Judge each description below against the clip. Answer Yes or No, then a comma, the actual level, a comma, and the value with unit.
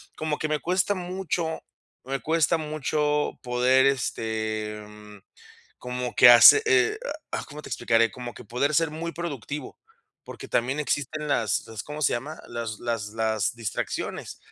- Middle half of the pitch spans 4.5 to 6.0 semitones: Yes, average, 5.2 semitones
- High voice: No, low, 135 Hz